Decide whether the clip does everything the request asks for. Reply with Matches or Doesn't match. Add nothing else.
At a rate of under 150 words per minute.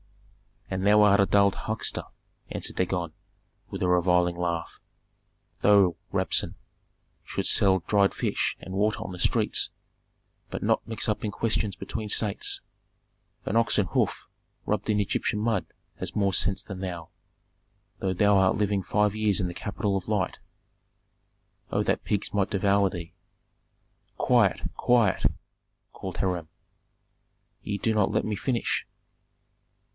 Matches